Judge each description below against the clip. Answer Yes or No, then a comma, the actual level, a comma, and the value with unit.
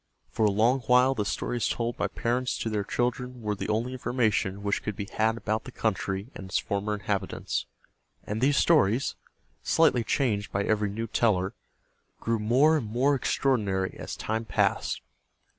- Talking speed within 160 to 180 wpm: Yes, average, 170 wpm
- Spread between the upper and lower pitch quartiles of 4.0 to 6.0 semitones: No, average, 3.3 semitones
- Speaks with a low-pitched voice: Yes, low, 110 Hz